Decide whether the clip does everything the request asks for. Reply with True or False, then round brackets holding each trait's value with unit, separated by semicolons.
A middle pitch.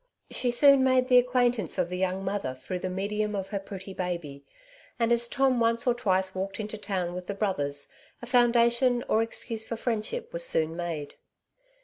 False (210 Hz)